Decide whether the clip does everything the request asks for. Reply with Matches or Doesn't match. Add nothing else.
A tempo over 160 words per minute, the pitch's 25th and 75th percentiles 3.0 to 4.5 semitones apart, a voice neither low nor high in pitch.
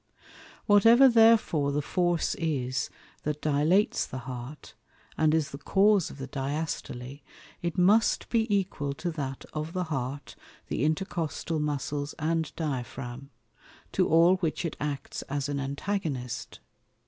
Doesn't match